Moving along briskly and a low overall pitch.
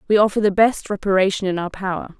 No: fast, 220 wpm; high, 195 Hz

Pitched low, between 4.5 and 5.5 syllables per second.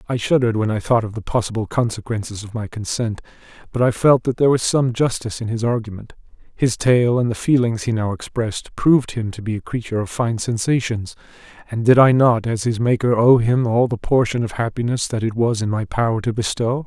No: low, 115 Hz; 5.8 syllables/s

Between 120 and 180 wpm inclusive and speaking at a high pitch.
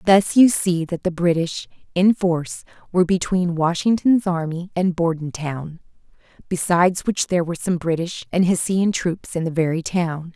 No: average, 155 wpm; medium, 175 Hz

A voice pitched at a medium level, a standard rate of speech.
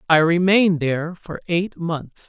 Yes: medium, 170 Hz; average, 160 wpm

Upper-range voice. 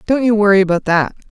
Yes: high, 205 Hz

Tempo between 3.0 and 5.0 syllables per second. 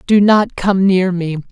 Yes: 4.0 syllables/s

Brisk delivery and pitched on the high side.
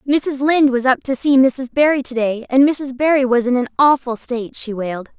Yes: fast, 220 wpm; very high, 260 Hz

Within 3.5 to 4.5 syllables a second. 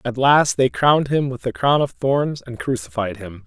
No: 4.8 syllables/s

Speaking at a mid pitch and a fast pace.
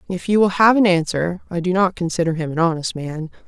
Yes: medium, 175 Hz; fast, 240 wpm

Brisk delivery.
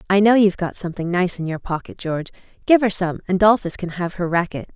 Yes: fast, 240 wpm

